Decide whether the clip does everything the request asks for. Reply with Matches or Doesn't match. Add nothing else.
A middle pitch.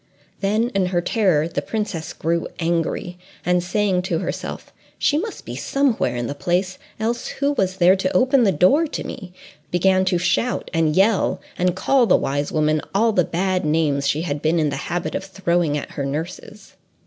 Matches